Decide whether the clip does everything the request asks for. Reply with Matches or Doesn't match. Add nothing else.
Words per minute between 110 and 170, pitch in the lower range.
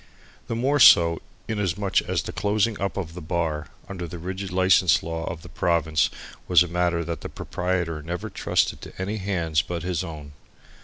Doesn't match